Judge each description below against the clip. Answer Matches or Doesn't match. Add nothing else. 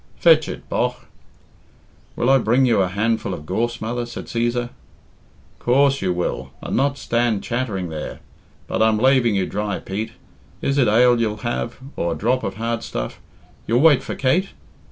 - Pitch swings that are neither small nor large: Matches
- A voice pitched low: Matches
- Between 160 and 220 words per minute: Matches